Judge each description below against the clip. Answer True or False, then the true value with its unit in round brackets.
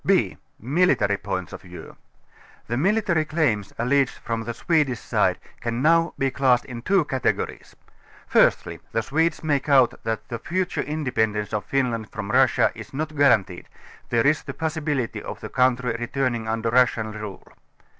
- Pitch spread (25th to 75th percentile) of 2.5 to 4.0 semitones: False (5.1 semitones)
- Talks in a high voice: False (125 Hz)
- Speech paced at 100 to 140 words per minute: False (165 wpm)